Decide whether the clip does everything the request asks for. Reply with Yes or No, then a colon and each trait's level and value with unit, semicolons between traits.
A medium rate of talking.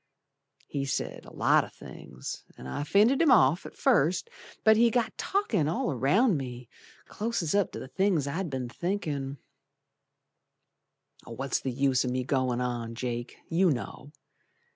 Yes: average, 155 wpm